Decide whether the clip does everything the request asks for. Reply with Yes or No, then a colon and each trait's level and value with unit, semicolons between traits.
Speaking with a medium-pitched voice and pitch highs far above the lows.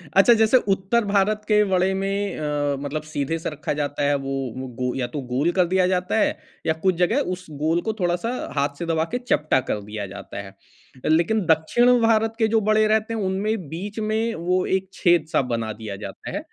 Yes: medium, 180 Hz; wide, 6.4 semitones